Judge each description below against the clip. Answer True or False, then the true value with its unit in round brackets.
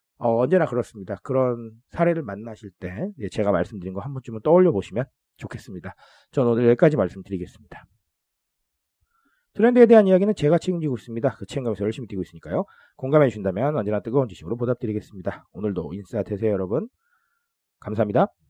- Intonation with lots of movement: True (7.2 semitones)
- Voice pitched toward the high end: False (120 Hz)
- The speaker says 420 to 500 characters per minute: True (430 characters per minute)